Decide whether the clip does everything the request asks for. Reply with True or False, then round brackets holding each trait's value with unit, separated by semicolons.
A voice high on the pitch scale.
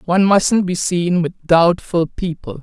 False (175 Hz)